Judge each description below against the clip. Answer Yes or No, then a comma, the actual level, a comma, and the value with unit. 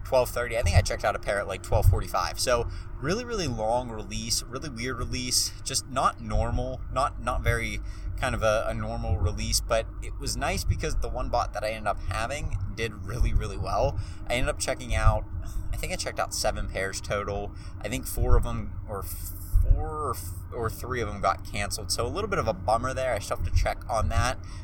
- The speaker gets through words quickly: Yes, fast, 220 wpm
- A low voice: Yes, low, 100 Hz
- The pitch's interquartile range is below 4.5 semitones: Yes, average, 3.3 semitones